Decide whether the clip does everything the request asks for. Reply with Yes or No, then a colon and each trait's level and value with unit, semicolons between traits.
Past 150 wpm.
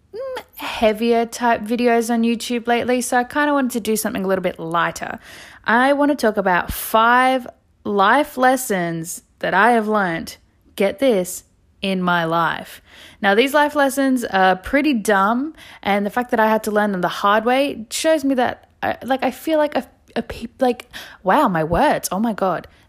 Yes: average, 190 wpm